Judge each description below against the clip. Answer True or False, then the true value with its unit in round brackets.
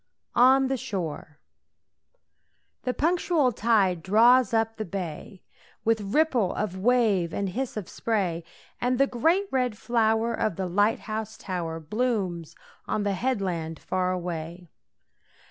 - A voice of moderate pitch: False (215 Hz)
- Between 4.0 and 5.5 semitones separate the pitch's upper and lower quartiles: True (5.1 semitones)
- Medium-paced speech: False (130 wpm)